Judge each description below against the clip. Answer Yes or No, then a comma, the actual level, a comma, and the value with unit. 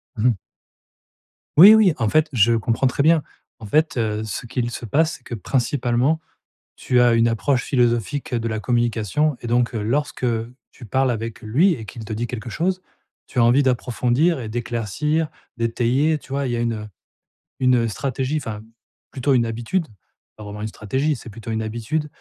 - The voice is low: Yes, low, 120 Hz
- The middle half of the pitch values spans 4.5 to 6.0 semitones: No, average, 3.7 semitones